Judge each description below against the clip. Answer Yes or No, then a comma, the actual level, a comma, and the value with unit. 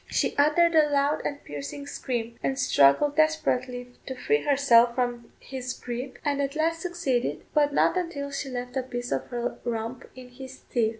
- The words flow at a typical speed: Yes, average, 180 wpm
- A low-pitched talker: No, very high, 265 Hz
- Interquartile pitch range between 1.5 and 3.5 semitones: Yes, average, 3.0 semitones